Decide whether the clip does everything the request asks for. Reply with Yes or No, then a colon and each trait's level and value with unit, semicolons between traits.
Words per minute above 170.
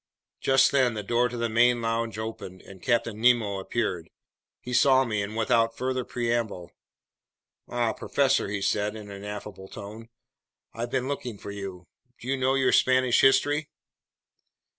No: average, 160 wpm